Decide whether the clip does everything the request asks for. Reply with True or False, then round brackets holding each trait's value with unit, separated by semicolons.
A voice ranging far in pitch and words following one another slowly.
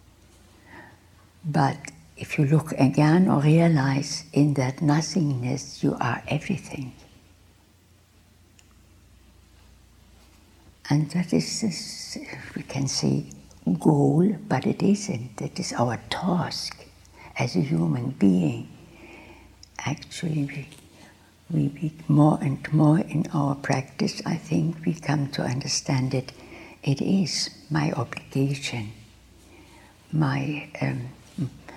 True (7.0 semitones; 105 wpm)